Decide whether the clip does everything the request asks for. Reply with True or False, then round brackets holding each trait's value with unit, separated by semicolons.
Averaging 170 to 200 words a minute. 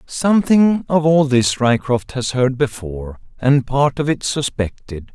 False (150 wpm)